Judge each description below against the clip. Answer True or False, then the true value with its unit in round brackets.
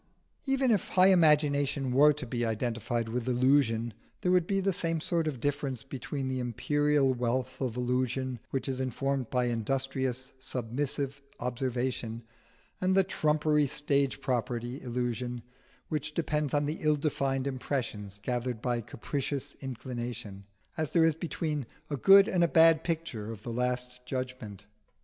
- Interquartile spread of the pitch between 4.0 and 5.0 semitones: False (3.5 semitones)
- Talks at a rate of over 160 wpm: False (150 wpm)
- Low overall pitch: True (130 Hz)